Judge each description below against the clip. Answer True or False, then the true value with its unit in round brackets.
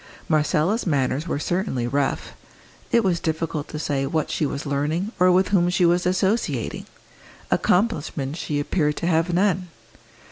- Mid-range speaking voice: True (165 Hz)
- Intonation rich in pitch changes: False (3.8 semitones)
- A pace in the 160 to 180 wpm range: False (150 wpm)